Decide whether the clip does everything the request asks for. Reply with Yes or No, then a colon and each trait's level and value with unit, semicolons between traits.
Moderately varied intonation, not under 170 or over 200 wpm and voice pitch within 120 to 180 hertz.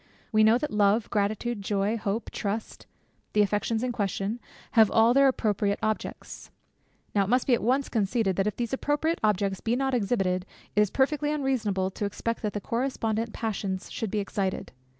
No: average, 3.2 semitones; average, 180 wpm; high, 215 Hz